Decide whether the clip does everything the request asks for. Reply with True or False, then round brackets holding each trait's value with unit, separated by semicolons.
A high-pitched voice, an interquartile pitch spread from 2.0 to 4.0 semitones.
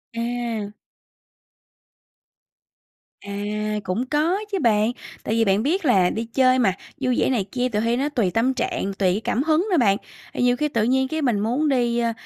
True (240 Hz; 3.7 semitones)